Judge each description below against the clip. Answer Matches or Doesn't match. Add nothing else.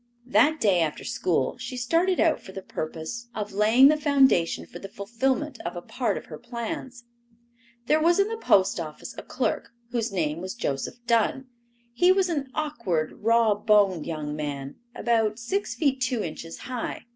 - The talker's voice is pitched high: Matches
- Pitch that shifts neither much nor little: Doesn't match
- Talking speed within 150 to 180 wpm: Matches